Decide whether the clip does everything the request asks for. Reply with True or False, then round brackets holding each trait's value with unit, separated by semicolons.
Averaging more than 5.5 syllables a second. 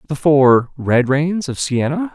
False (3.7 syllables/s)